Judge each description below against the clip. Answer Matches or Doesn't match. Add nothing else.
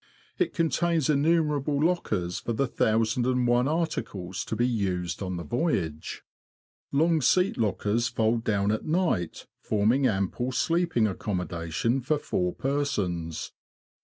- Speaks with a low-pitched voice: Matches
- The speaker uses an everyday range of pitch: Doesn't match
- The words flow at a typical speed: Doesn't match